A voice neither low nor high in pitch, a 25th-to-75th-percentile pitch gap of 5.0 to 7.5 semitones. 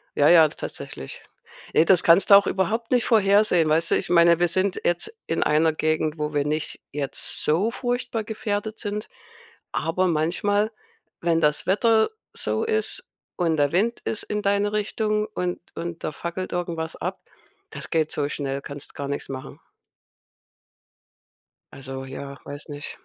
Yes: medium, 170 Hz; average, 5.3 semitones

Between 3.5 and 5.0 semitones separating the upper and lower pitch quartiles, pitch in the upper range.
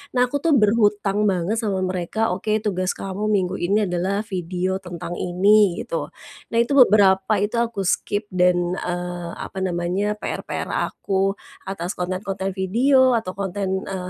No: narrow, 2.5 semitones; high, 195 Hz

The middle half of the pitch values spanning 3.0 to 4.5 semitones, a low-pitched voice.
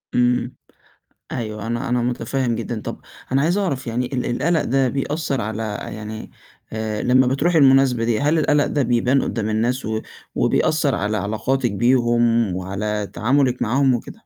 Yes: average, 3.5 semitones; low, 120 Hz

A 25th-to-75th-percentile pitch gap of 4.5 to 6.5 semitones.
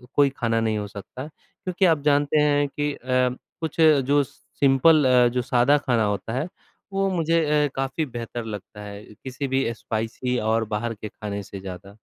Yes: average, 4.9 semitones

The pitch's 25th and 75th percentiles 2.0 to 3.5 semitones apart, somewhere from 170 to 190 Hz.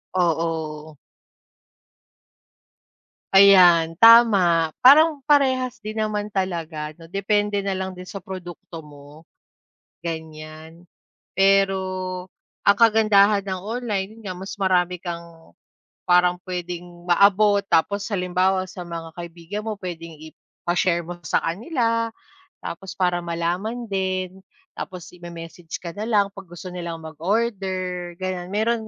Yes: average, 3.1 semitones; medium, 185 Hz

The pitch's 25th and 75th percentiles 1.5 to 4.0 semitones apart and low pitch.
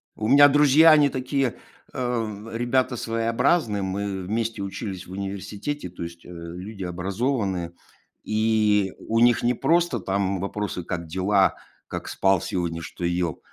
No: average, 4.5 semitones; low, 105 Hz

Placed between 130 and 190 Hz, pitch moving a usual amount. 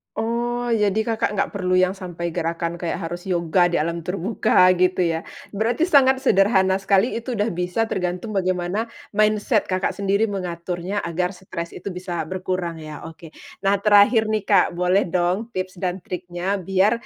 Yes: medium, 185 Hz; average, 3.1 semitones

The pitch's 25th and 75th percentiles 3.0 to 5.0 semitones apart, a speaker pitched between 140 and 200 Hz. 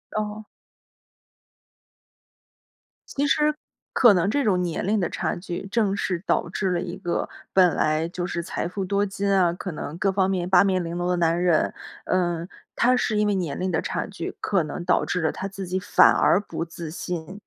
No: narrow, 2.4 semitones; medium, 185 Hz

